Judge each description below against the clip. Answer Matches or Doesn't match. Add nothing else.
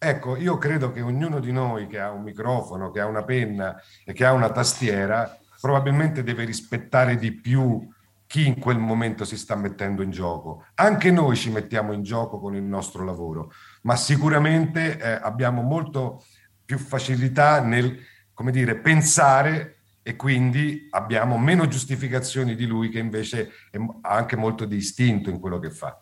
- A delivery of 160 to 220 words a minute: Matches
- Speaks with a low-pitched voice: Matches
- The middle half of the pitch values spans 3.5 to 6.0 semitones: Matches